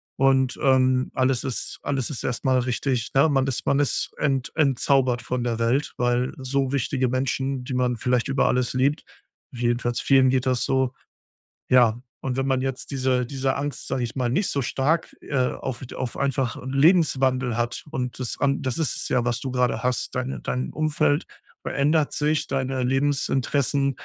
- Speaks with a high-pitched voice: No, low, 130 Hz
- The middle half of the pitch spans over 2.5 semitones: No, narrow, 1.7 semitones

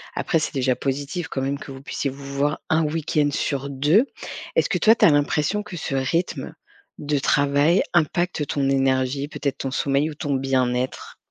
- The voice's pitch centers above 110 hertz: Yes, medium, 140 Hz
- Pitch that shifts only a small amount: Yes, narrow, 2.3 semitones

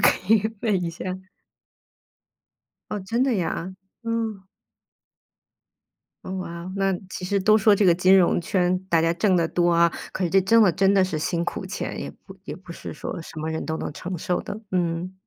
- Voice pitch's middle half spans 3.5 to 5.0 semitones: No, average, 2.7 semitones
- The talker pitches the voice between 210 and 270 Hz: No, medium, 185 Hz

